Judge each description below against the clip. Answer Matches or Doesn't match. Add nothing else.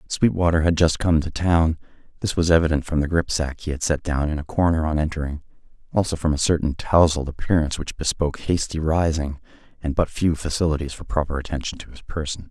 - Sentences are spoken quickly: Doesn't match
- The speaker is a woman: Doesn't match